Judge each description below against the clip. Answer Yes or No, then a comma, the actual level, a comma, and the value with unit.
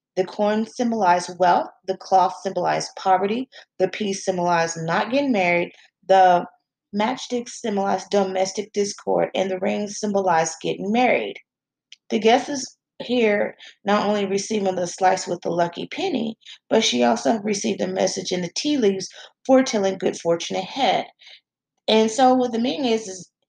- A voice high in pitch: Yes, high, 195 Hz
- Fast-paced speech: No, average, 150 wpm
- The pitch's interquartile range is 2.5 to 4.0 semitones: Yes, average, 3.3 semitones